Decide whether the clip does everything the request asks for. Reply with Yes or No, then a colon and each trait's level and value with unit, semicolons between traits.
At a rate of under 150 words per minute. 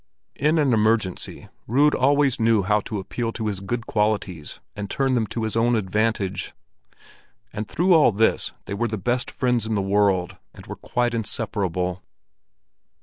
No: average, 165 wpm